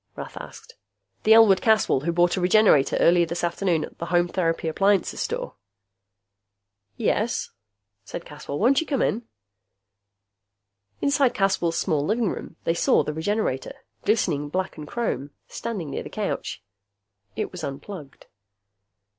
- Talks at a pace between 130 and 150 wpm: Yes, average, 140 wpm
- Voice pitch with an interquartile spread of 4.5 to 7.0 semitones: Yes, average, 5.1 semitones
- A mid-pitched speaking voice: Yes, medium, 180 Hz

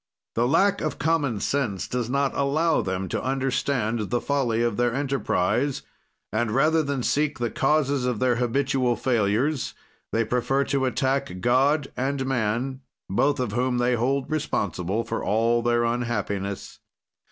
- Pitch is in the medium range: No, low, 125 Hz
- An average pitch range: Yes, average, 3.1 semitones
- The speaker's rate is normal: Yes, average, 150 wpm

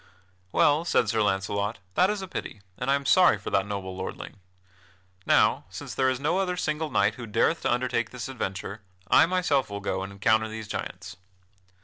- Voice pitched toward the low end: Yes, low, 115 Hz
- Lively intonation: Yes, wide, 6.6 semitones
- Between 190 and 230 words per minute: Yes, average, 195 wpm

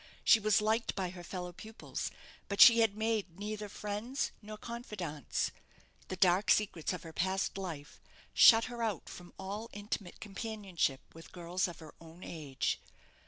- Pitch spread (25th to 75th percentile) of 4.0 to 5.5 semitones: No, average, 3.6 semitones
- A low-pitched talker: No, high, 195 Hz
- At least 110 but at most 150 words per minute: No, average, 160 wpm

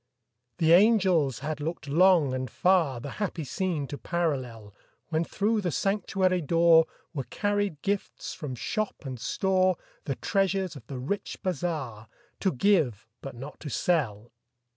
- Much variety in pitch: Yes, wide, 5.7 semitones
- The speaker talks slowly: No, average, 145 wpm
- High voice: No, medium, 165 Hz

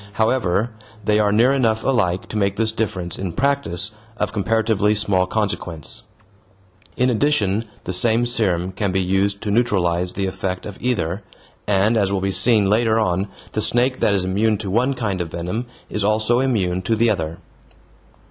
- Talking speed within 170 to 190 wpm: Yes, average, 175 wpm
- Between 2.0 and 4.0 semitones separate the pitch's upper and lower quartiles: Yes, average, 3.3 semitones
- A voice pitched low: Yes, low, 105 Hz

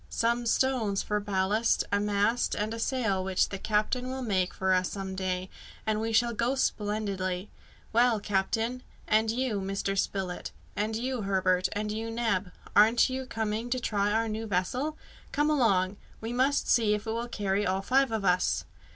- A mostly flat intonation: No, average, 3.3 semitones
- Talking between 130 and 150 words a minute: No, average, 175 wpm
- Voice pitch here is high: Yes, high, 215 Hz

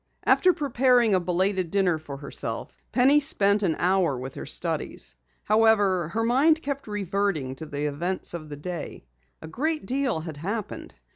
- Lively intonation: Yes, wide, 7.0 semitones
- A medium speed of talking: Yes, average, 160 wpm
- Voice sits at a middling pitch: No, high, 195 Hz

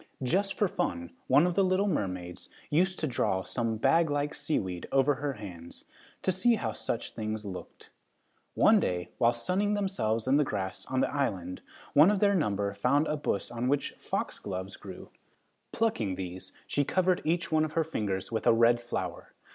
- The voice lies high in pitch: No, low, 130 Hz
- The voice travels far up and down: Yes, wide, 8.6 semitones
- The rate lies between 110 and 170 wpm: No, average, 180 wpm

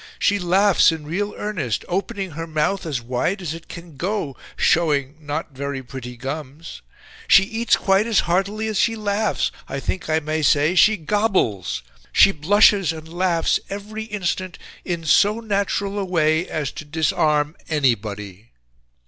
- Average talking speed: Yes, average, 155 wpm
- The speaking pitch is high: No, medium, 165 Hz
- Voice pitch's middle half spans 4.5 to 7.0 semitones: Yes, average, 5.3 semitones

